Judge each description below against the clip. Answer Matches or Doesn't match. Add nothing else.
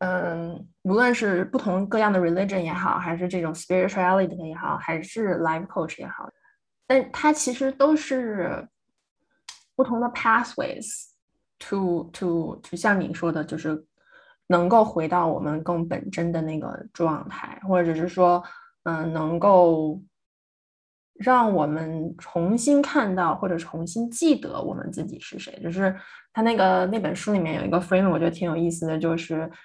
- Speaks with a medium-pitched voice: Matches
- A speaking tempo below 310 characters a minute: Matches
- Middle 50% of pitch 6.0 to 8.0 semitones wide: Doesn't match